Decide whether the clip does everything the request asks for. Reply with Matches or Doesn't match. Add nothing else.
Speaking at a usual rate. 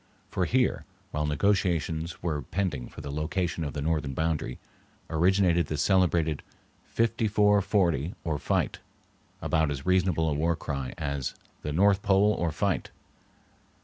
Matches